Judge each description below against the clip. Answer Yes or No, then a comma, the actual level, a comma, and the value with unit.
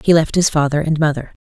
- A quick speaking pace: Yes, fast, 250 wpm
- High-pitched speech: No, medium, 155 Hz